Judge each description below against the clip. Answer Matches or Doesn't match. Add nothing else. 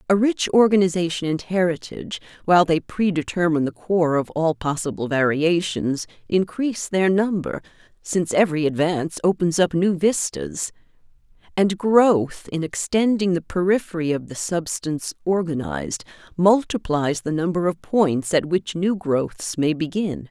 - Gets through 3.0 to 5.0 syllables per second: Matches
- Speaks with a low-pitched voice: Doesn't match